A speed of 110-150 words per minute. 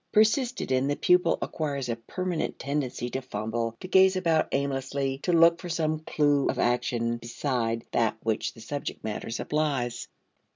No: average, 160 wpm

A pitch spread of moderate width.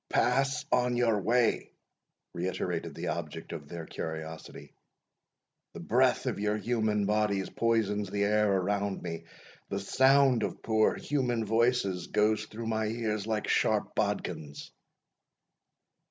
Yes: average, 3.1 semitones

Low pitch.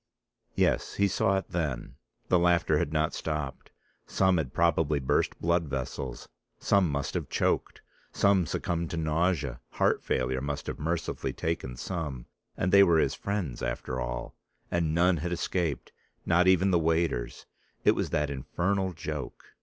Yes: very low, 80 Hz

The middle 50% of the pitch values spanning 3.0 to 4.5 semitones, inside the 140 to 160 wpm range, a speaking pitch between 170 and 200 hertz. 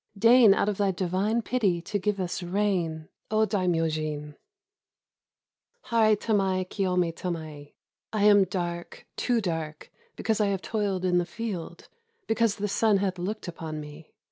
Yes: average, 3.5 semitones; average, 150 wpm; high, 190 Hz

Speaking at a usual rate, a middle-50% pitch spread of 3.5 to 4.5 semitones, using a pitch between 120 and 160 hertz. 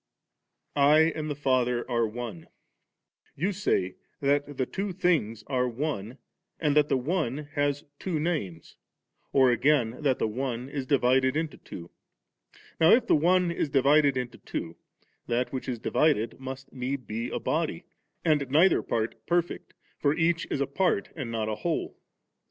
Yes: average, 160 wpm; average, 4.1 semitones; medium, 140 Hz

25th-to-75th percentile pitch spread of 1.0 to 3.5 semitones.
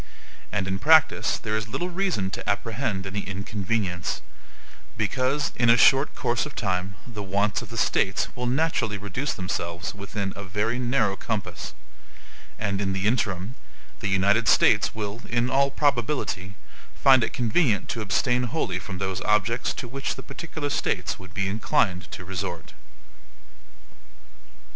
No: average, 4.2 semitones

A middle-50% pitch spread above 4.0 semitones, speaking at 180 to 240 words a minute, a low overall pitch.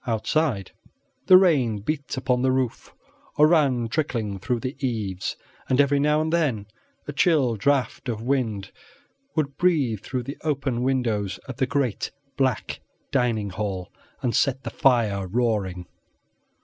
No: average, 4.4 semitones; average, 145 wpm; low, 125 Hz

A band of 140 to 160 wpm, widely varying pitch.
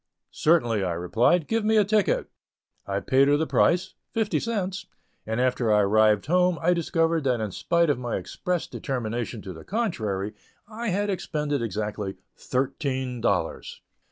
Yes: average, 155 wpm; wide, 8.6 semitones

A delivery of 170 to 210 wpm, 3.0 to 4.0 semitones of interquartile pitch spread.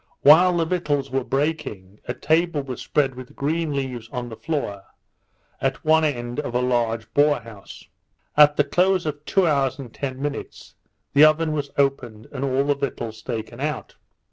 Yes: average, 175 wpm; average, 3.7 semitones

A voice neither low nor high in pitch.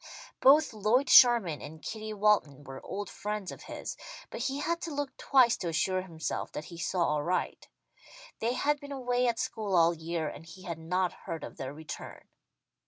No: high, 195 Hz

